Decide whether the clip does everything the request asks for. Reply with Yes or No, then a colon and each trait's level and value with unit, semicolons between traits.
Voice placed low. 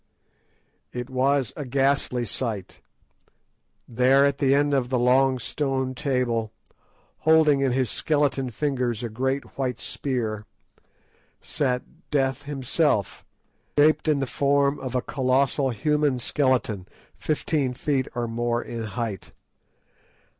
Yes: low, 130 Hz